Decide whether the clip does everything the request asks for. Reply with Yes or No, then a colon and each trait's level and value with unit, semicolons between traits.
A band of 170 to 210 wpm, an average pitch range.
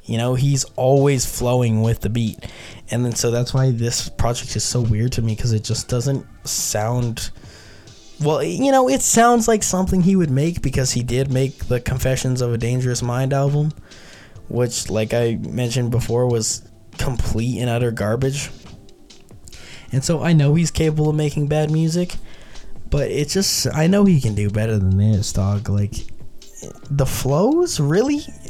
Yes: average, 175 wpm; average, 4.5 semitones